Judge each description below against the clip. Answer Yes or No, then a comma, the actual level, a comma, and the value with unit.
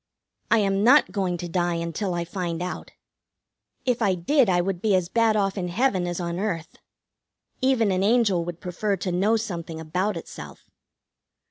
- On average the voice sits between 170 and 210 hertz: Yes, medium, 185 Hz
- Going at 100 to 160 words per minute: No, average, 175 wpm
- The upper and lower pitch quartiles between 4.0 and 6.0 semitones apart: No, average, 3.5 semitones